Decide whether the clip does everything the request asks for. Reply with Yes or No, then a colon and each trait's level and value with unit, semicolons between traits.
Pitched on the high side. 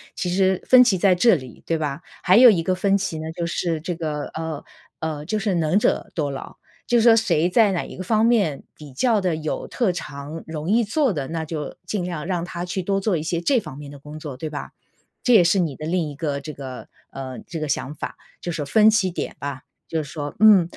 No: medium, 170 Hz